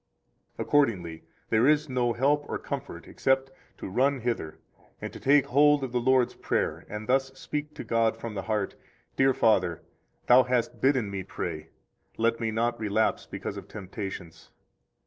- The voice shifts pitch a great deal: No, average, 4.0 semitones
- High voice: No, low, 120 Hz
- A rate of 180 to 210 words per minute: No, average, 165 wpm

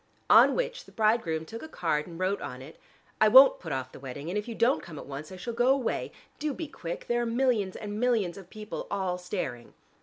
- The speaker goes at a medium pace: No, fast, 240 wpm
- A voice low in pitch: No, high, 200 Hz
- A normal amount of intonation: No, wide, 6.7 semitones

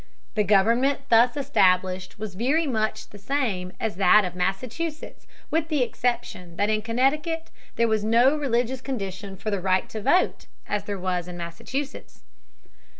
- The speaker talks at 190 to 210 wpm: No, average, 155 wpm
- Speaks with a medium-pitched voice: No, high, 220 Hz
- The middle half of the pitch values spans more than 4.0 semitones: Yes, wide, 5.5 semitones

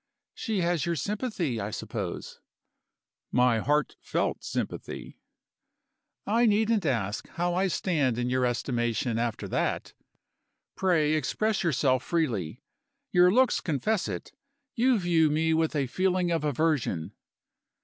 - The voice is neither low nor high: Yes, medium, 155 Hz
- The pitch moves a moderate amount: No, wide, 6.9 semitones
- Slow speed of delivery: Yes, slow, 125 wpm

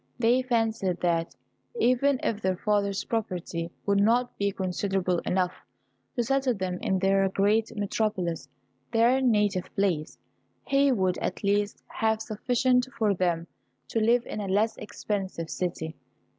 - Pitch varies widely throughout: No, average, 3.6 semitones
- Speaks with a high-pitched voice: Yes, high, 205 Hz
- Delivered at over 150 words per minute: No, average, 140 wpm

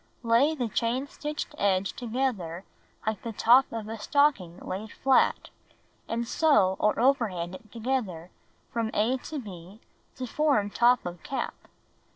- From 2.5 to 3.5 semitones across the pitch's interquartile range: No, average, 4.9 semitones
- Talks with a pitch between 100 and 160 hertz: No, high, 230 Hz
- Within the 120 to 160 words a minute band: Yes, average, 145 wpm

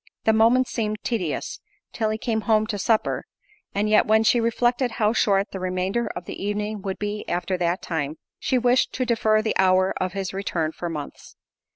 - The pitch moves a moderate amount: Yes, average, 3.2 semitones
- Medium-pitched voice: No, high, 210 Hz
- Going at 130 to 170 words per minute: No, average, 195 wpm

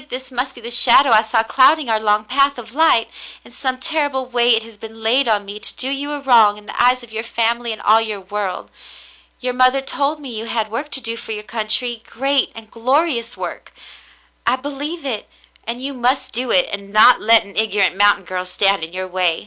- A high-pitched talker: Yes, high, 235 Hz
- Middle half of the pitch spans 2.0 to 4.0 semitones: Yes, average, 3.4 semitones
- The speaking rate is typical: No, fast, 225 wpm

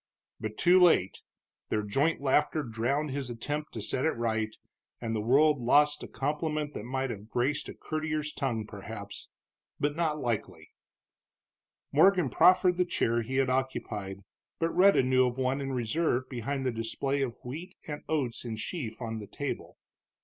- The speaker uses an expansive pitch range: No, average, 4.7 semitones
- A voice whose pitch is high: No, low, 130 Hz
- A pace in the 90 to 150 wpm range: No, average, 165 wpm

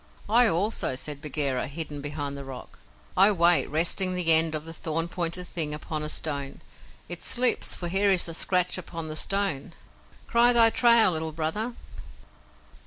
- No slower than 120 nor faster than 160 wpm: No, average, 170 wpm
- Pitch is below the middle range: No, medium, 165 Hz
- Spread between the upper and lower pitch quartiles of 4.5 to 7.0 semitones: No, average, 4.1 semitones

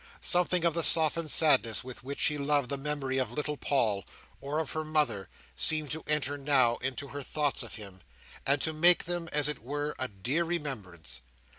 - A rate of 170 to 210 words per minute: Yes, average, 190 wpm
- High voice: No, medium, 145 Hz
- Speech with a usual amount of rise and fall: Yes, average, 3.3 semitones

